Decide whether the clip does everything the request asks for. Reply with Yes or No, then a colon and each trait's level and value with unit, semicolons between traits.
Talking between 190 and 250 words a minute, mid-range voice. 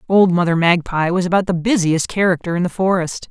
Yes: average, 200 wpm; medium, 180 Hz